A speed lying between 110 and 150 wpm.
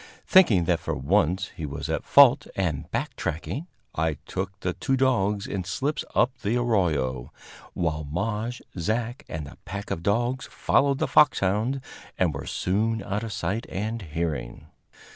No: average, 160 wpm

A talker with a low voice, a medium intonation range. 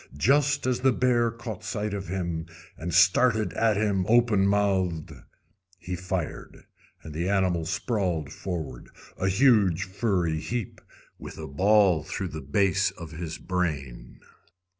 Yes: very low, 95 Hz; average, 4.2 semitones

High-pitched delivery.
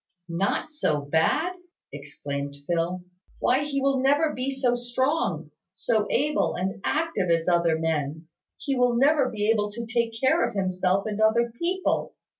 Yes: high, 220 Hz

